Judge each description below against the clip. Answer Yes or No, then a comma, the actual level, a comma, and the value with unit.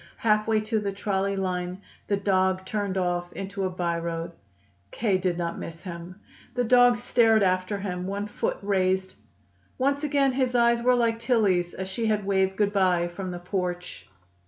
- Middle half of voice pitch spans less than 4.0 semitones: Yes, average, 3.3 semitones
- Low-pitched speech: No, high, 195 Hz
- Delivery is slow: No, average, 175 wpm